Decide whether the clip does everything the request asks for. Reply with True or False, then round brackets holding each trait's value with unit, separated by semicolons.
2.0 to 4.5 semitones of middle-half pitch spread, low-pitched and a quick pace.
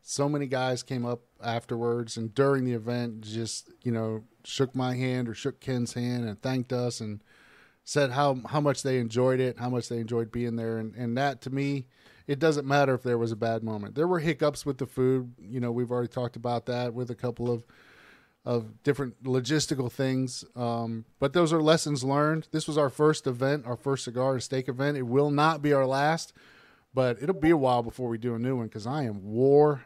True (2.9 semitones; 125 Hz; 220 wpm)